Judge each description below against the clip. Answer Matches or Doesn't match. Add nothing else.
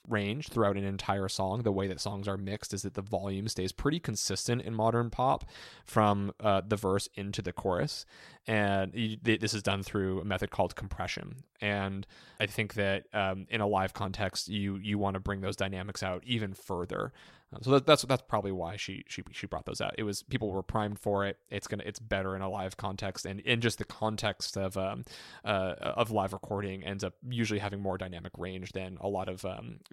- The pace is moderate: Doesn't match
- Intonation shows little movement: Matches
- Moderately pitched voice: Doesn't match